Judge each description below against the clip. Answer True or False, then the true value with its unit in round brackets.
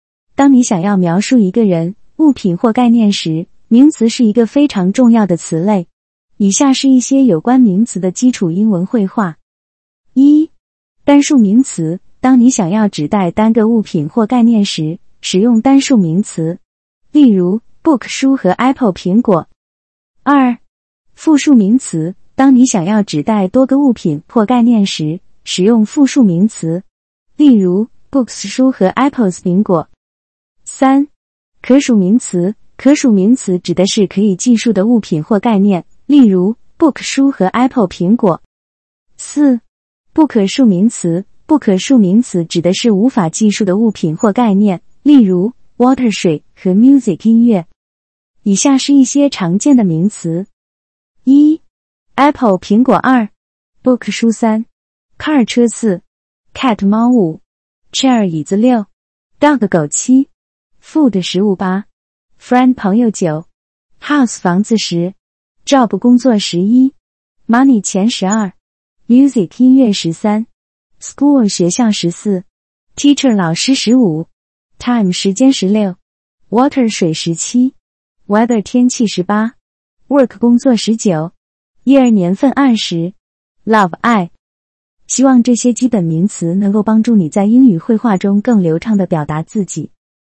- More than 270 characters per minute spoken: False (260 characters per minute)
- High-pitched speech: True (215 Hz)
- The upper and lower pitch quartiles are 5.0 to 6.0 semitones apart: True (5.4 semitones)